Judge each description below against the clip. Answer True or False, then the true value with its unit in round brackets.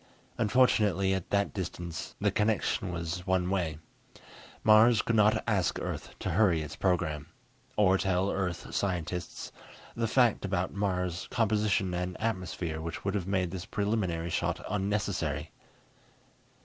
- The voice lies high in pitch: False (95 Hz)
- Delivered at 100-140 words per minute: True (135 wpm)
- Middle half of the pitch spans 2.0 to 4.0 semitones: True (3.0 semitones)